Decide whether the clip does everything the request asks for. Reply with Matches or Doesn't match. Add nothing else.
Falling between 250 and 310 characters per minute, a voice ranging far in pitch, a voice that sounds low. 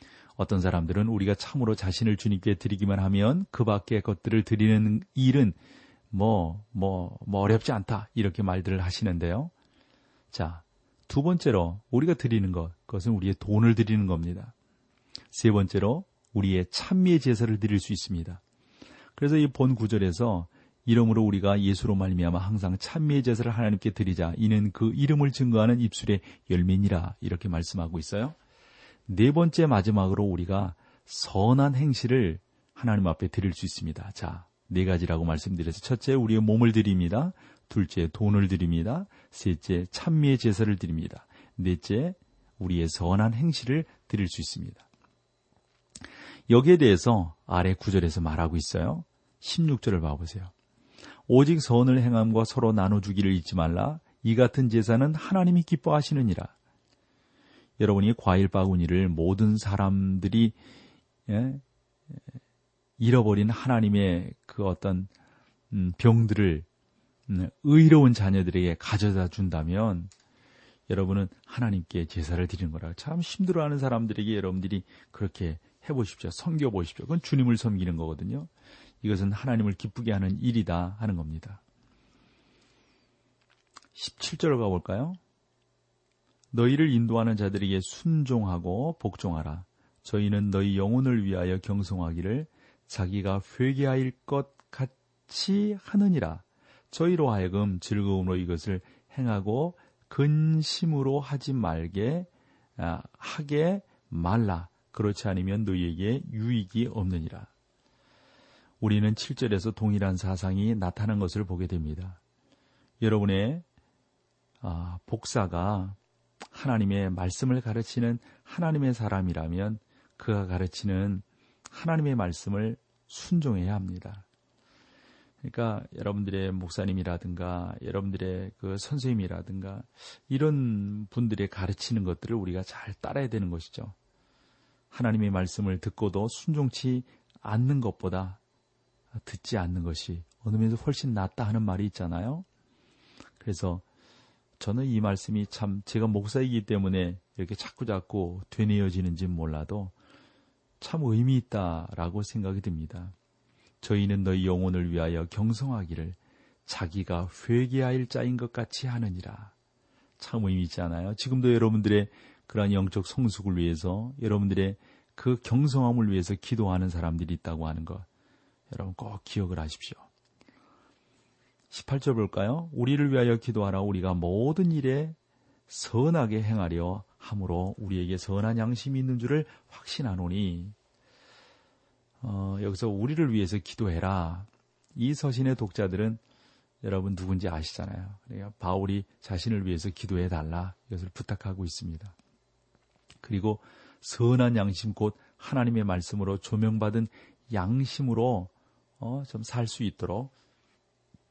Doesn't match